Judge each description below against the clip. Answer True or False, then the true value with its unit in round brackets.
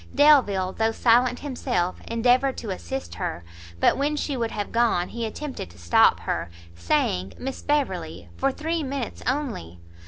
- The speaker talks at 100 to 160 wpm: True (155 wpm)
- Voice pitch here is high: True (240 Hz)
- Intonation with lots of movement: True (6.7 semitones)